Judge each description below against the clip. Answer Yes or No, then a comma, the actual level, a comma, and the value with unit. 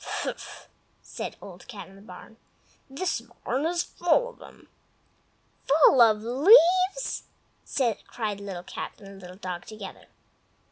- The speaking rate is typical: No, slow, 130 wpm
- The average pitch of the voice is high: Yes, high, 230 Hz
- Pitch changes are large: Yes, wide, 9.0 semitones